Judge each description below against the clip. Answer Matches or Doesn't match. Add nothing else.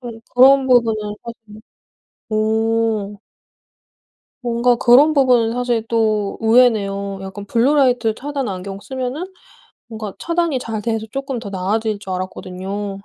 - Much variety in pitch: Doesn't match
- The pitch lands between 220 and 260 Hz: Matches